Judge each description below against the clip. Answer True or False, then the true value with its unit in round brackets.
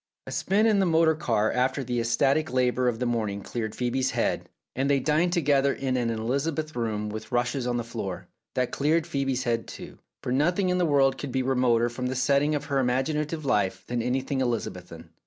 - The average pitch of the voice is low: True (130 Hz)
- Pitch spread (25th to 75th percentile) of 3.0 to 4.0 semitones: True (3.5 semitones)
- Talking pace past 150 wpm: True (205 wpm)